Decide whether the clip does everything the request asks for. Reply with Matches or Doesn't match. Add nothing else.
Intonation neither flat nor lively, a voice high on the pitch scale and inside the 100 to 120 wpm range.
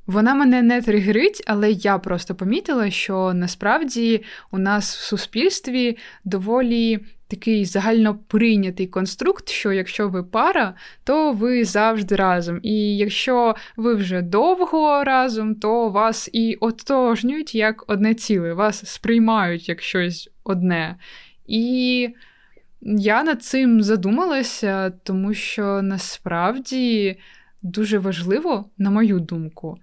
Matches